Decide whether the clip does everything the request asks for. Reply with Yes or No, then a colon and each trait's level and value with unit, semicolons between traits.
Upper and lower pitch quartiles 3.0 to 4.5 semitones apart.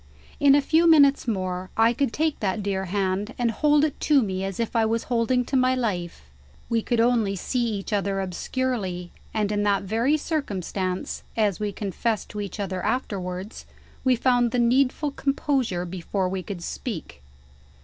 No: average, 4.9 semitones